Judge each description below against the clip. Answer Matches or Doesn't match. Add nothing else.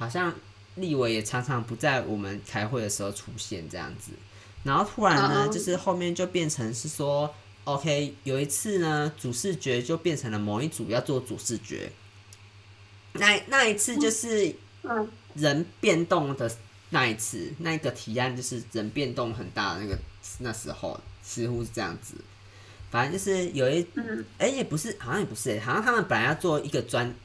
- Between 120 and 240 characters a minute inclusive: Doesn't match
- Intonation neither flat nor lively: Doesn't match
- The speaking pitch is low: Matches